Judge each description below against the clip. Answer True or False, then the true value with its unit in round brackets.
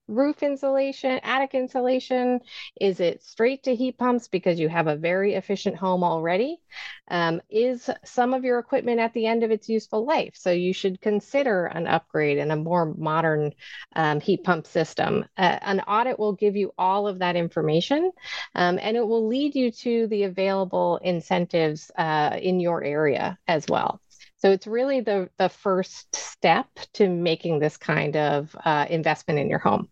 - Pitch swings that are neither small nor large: False (6.5 semitones)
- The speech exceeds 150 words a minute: True (175 wpm)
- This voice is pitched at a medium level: False (195 Hz)